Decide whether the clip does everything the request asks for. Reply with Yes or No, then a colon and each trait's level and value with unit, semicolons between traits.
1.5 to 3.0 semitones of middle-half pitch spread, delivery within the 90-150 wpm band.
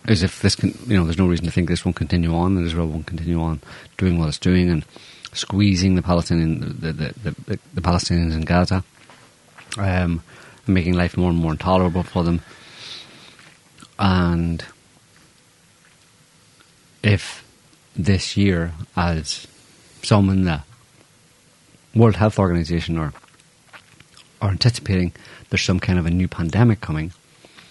Yes: average, 2.7 semitones; average, 145 wpm